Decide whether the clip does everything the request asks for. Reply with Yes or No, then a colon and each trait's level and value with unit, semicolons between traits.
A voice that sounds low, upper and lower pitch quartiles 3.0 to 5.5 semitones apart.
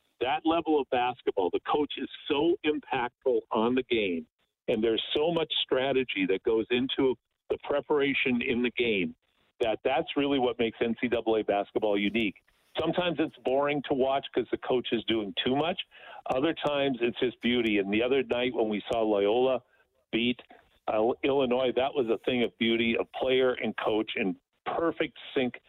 Yes: low, 130 Hz; average, 4.1 semitones